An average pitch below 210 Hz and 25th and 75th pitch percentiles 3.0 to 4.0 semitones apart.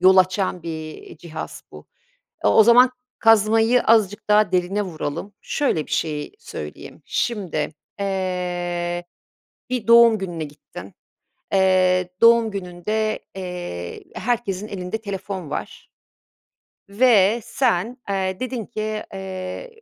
Yes: high, 190 Hz; average, 3.7 semitones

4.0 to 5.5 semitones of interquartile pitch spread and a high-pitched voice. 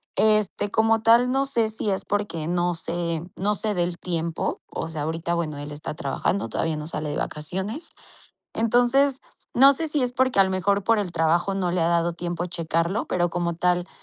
No: average, 4.6 semitones; medium, 180 Hz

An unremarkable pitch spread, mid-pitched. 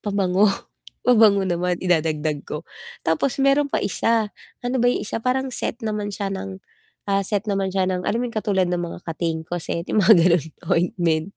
No: average, 3.7 semitones; high, 195 Hz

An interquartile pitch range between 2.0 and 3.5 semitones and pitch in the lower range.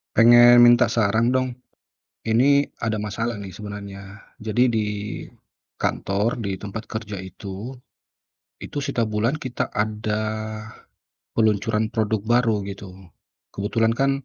Yes: narrow, 2.6 semitones; low, 110 Hz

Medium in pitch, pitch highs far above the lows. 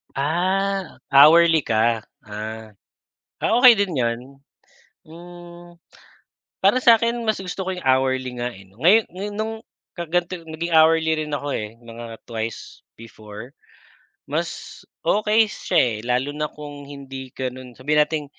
Yes: medium, 150 Hz; wide, 6.3 semitones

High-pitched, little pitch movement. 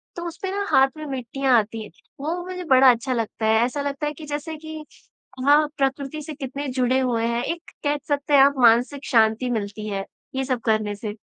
No: very high, 265 Hz; average, 4.1 semitones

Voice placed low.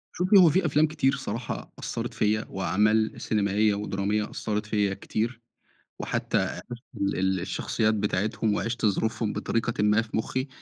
Yes: low, 110 Hz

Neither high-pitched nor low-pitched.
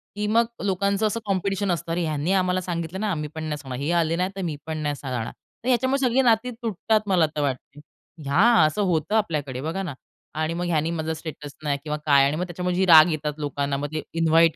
Yes: medium, 165 Hz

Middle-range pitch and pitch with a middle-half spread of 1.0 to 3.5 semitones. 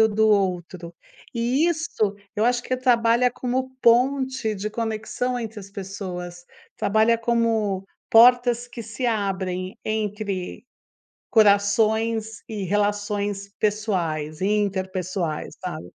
No: high, 215 Hz; average, 3.1 semitones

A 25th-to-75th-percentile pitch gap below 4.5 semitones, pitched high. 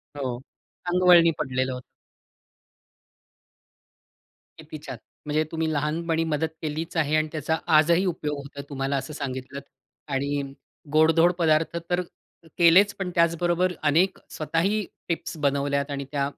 No: average, 3.0 semitones; medium, 155 Hz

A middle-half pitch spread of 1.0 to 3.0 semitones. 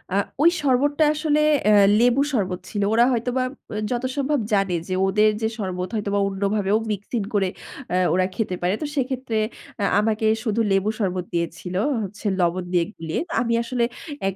No: average, 4.8 semitones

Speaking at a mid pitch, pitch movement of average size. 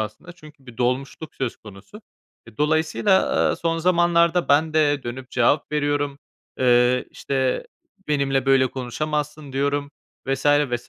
Yes: medium, 145 Hz; average, 3.1 semitones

